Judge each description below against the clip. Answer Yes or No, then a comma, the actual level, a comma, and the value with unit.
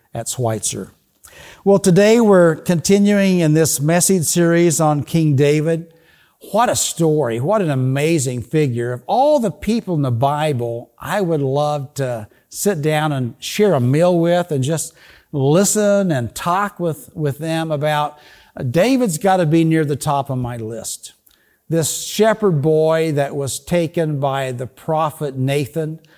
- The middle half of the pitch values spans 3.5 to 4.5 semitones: Yes, average, 3.8 semitones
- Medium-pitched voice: Yes, medium, 155 Hz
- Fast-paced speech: No, average, 155 wpm